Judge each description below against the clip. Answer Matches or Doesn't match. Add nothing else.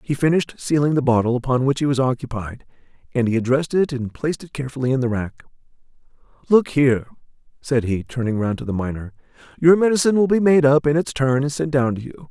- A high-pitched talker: Doesn't match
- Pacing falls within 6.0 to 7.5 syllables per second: Matches